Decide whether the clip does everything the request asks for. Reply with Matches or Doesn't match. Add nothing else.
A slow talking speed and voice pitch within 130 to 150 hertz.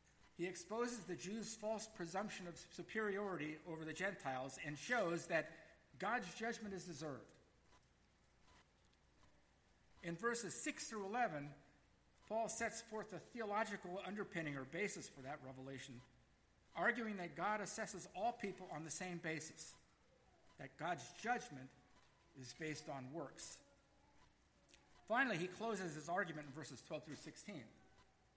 Doesn't match